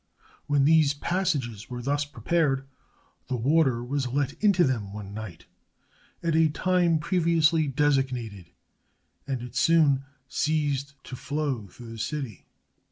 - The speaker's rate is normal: No, slow, 130 wpm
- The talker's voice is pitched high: No, medium, 140 Hz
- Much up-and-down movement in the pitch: No, average, 4.3 semitones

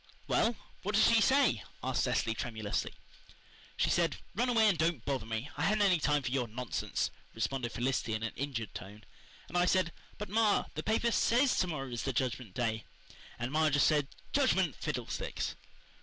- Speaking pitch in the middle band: Yes, medium, 145 Hz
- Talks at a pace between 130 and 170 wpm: No, average, 185 wpm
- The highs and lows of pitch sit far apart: Yes, wide, 9.0 semitones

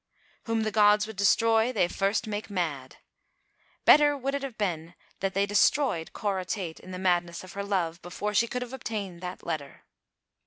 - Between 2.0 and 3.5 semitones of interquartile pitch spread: No, average, 3.9 semitones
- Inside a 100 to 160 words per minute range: No, average, 190 wpm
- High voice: Yes, high, 200 Hz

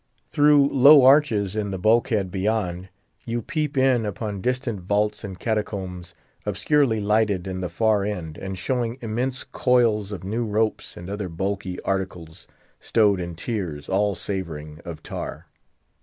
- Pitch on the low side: Yes, low, 105 Hz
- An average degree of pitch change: Yes, average, 4.1 semitones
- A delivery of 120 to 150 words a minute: Yes, average, 145 wpm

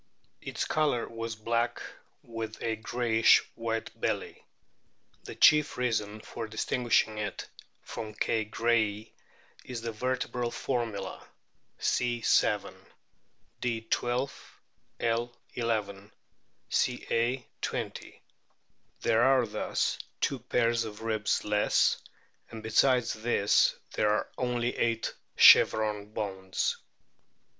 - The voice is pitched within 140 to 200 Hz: No, low, 115 Hz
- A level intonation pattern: Yes, narrow, 1.9 semitones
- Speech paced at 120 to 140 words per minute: No, slow, 100 wpm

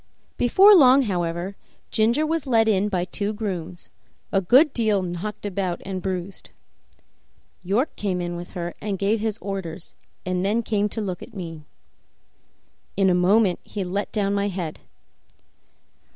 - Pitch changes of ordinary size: Yes, average, 3.3 semitones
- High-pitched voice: Yes, high, 200 Hz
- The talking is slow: No, average, 150 wpm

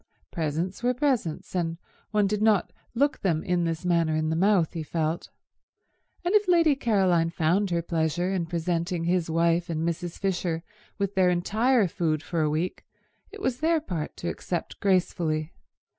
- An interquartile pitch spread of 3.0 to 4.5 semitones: Yes, average, 3.5 semitones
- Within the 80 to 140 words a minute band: No, average, 170 wpm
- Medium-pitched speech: Yes, medium, 175 Hz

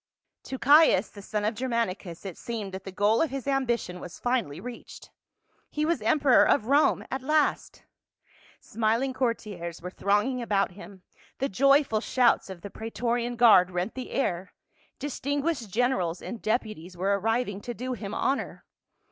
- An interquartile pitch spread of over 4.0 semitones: Yes, average, 4.8 semitones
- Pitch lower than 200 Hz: No, high, 230 Hz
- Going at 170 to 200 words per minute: No, average, 160 wpm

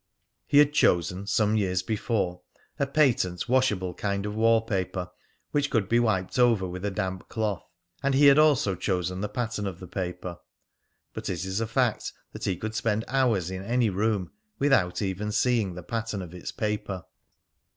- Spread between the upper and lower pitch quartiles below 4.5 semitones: Yes, average, 3.9 semitones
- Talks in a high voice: No, low, 105 Hz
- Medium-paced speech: Yes, average, 180 wpm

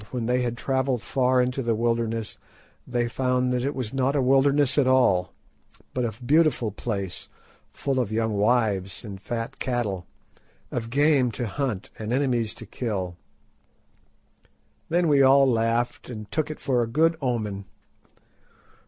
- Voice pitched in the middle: No, low, 120 Hz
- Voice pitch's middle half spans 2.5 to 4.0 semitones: Yes, average, 2.9 semitones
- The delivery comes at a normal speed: Yes, average, 155 wpm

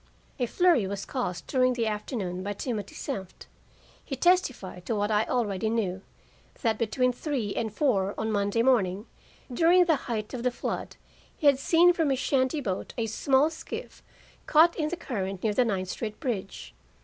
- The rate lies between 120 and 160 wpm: No, average, 175 wpm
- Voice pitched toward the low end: No, high, 230 Hz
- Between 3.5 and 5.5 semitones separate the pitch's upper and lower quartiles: Yes, average, 5.0 semitones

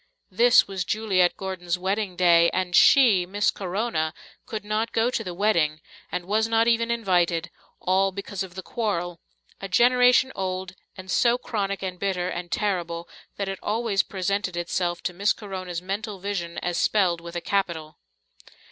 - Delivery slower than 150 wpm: No, average, 165 wpm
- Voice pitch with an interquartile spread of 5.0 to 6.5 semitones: No, average, 3.1 semitones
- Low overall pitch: No, high, 190 Hz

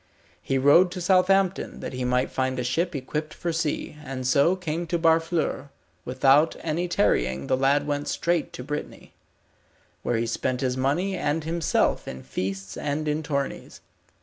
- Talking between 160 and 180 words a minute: Yes, average, 165 wpm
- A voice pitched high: No, medium, 145 Hz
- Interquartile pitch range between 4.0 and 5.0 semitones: Yes, average, 4.5 semitones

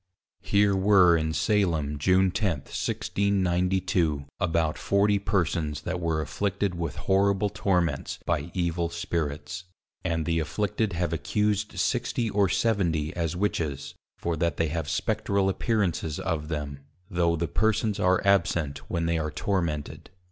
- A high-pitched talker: No, very low, 85 Hz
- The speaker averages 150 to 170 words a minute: No, slow, 135 wpm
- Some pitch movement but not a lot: Yes, average, 3.8 semitones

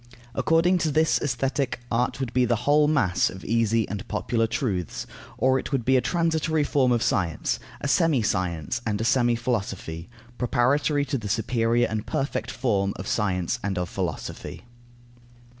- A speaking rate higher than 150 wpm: Yes, average, 165 wpm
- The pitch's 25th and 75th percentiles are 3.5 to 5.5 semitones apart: Yes, average, 5.2 semitones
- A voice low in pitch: Yes, low, 120 Hz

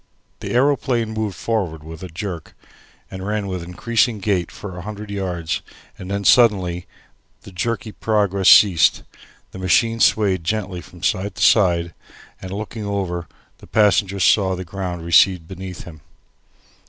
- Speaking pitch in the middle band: No, very low, 95 Hz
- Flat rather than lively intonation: No, average, 3.2 semitones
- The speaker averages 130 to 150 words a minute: Yes, average, 145 wpm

